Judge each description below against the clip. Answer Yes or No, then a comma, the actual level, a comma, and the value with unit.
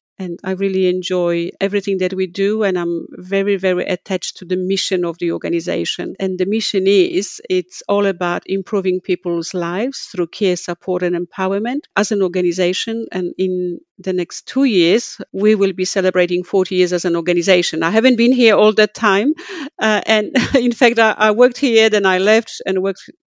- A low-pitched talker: No, high, 190 Hz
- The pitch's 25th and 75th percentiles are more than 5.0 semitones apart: No, average, 3.0 semitones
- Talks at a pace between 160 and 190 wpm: Yes, average, 185 wpm